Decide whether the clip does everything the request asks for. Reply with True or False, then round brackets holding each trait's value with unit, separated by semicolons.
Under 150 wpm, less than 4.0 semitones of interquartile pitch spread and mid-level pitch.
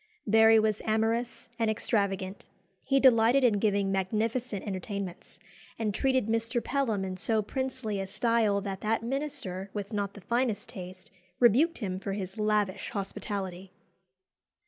False (140 wpm; 2.9 semitones; 215 Hz)